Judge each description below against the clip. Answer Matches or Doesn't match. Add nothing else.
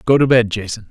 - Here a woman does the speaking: Doesn't match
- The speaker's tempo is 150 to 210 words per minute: Doesn't match